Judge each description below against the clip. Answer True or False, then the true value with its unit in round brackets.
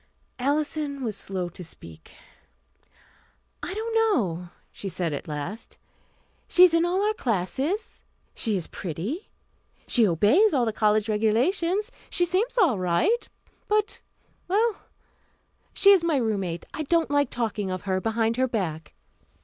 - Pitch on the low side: False (240 Hz)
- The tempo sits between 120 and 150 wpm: True (140 wpm)